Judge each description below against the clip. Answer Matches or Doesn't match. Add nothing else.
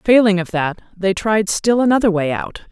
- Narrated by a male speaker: Doesn't match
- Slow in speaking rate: Doesn't match